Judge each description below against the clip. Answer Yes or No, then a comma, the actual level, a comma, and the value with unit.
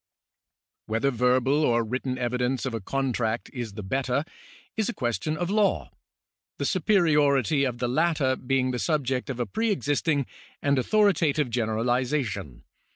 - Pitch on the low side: Yes, low, 130 Hz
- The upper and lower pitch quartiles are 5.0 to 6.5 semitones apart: No, average, 3.7 semitones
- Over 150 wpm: No, average, 145 wpm